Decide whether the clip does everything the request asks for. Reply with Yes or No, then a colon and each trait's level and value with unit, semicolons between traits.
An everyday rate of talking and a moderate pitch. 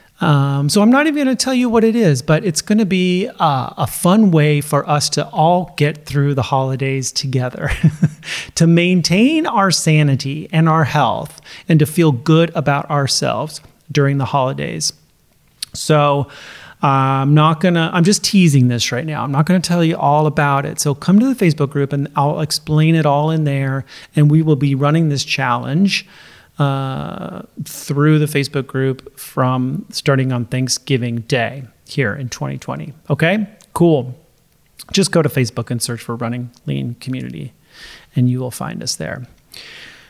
Yes: average, 175 wpm; medium, 150 Hz